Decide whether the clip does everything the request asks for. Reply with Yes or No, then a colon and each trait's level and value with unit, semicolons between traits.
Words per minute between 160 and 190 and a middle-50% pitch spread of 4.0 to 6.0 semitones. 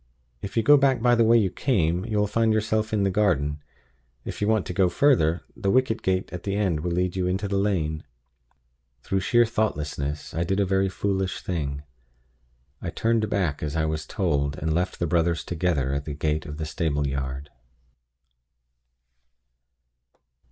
Yes: average, 180 wpm; average, 5.3 semitones